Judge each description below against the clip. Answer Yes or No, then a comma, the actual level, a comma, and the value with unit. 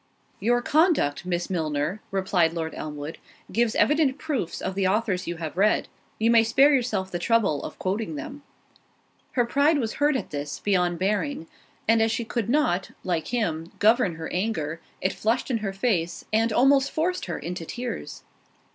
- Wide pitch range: Yes, wide, 5.9 semitones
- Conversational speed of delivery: Yes, average, 175 wpm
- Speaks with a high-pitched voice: Yes, high, 210 Hz